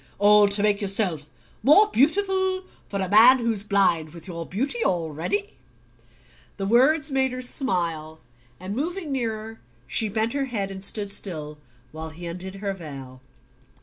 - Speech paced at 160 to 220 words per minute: No, average, 150 wpm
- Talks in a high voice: Yes, high, 205 Hz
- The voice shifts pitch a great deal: Yes, wide, 6.6 semitones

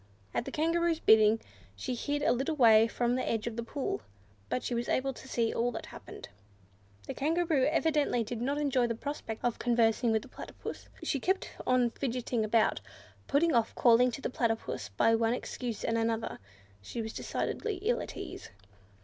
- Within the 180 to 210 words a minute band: Yes, average, 185 wpm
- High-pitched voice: Yes, high, 240 Hz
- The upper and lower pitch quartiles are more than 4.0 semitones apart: No, average, 3.7 semitones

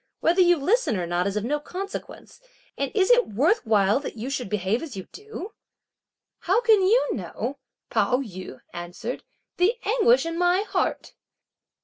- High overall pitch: Yes, very high, 315 Hz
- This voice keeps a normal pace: Yes, average, 165 wpm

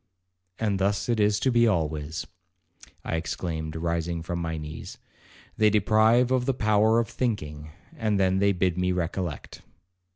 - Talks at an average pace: Yes, average, 155 wpm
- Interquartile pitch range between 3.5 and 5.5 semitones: Yes, average, 4.9 semitones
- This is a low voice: Yes, very low, 95 Hz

